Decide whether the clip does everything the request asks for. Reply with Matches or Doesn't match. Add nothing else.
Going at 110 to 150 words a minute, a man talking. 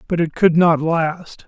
Doesn't match